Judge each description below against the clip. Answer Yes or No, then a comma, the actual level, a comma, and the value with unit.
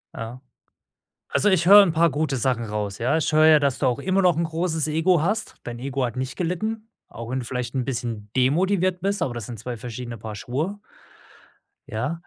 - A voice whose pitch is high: No, medium, 140 Hz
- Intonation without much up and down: No, wide, 6.0 semitones